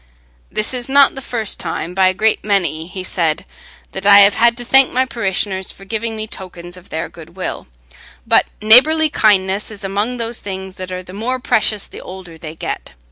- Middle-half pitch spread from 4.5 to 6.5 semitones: No, average, 3.8 semitones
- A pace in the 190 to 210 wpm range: Yes, average, 195 wpm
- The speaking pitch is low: No, high, 200 Hz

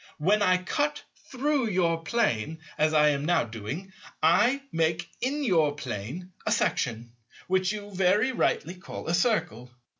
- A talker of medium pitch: Yes, medium, 180 Hz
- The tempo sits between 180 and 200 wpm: No, average, 150 wpm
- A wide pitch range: Yes, wide, 6.0 semitones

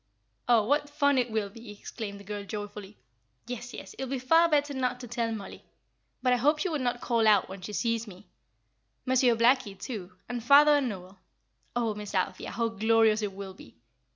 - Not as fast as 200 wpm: No, fast, 205 wpm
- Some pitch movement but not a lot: Yes, average, 3.7 semitones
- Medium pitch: No, high, 230 Hz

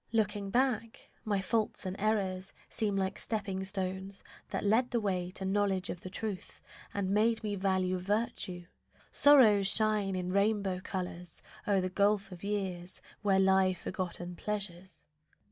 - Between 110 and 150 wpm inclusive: Yes, average, 145 wpm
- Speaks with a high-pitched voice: Yes, high, 195 Hz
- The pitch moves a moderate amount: No, narrow, 2.1 semitones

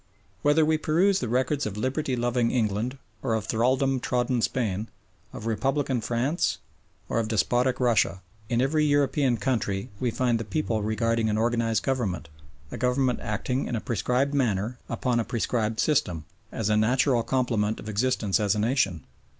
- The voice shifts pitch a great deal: No, average, 3.3 semitones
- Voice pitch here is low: Yes, low, 120 Hz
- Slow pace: No, average, 165 wpm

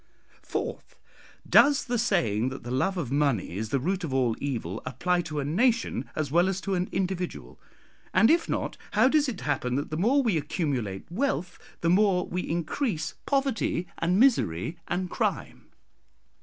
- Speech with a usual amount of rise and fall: No, wide, 7.0 semitones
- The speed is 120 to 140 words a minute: No, average, 170 wpm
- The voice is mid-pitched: Yes, medium, 175 Hz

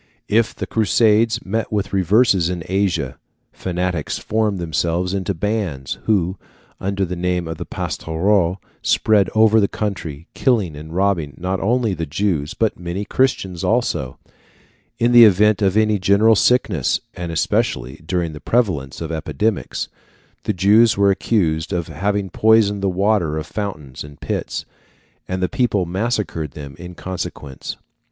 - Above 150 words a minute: No, average, 145 wpm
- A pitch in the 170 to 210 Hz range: No, very low, 95 Hz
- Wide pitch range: No, average, 4.2 semitones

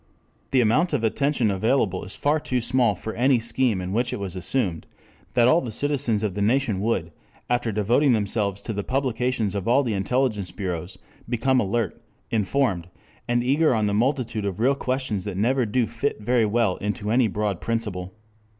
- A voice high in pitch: No, low, 115 Hz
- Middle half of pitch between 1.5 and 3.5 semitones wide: No, average, 4.0 semitones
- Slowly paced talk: No, average, 185 wpm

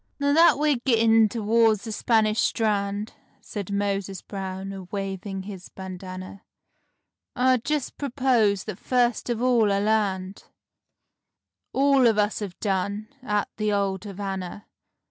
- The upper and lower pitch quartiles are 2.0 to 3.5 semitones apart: Yes, average, 3.1 semitones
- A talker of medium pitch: No, high, 210 Hz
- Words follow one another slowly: Yes, slow, 130 wpm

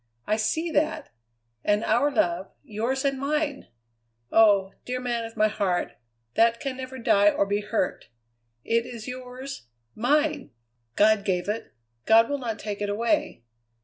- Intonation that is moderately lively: Yes, average, 4.3 semitones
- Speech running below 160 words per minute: Yes, average, 150 wpm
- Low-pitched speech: No, high, 230 Hz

